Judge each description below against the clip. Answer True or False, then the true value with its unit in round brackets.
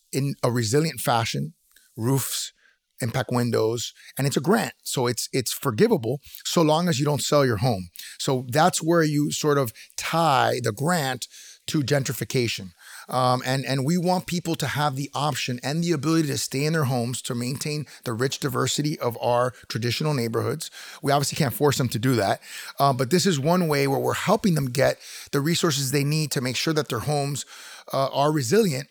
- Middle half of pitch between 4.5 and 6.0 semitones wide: False (3.5 semitones)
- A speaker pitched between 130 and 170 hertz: True (140 Hz)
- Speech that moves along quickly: False (195 wpm)